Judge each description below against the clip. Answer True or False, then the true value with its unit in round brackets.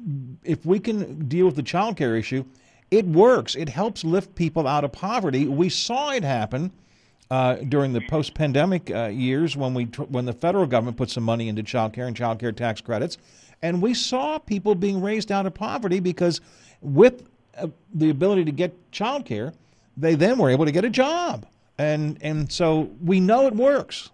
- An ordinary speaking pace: True (195 wpm)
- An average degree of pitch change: False (6.7 semitones)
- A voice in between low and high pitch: True (160 Hz)